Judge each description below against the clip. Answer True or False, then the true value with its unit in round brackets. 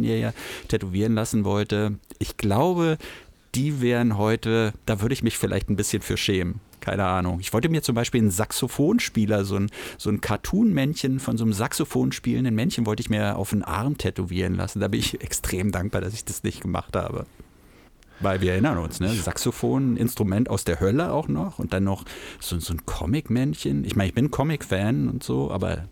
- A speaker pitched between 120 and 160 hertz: False (105 Hz)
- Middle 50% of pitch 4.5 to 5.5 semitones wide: False (4.0 semitones)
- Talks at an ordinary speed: False (200 wpm)